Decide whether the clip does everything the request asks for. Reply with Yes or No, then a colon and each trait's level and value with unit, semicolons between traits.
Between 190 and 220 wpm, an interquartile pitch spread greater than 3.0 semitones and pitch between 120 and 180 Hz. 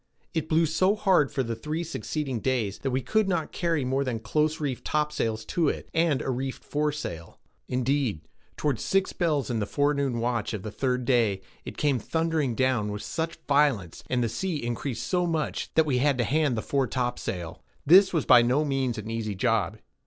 Yes: average, 195 wpm; average, 4.7 semitones; low, 135 Hz